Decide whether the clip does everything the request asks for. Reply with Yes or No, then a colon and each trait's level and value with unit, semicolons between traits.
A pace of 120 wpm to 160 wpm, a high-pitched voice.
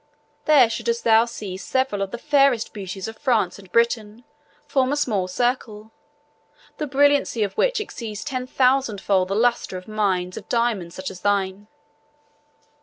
Yes: average, 155 wpm; high, 225 Hz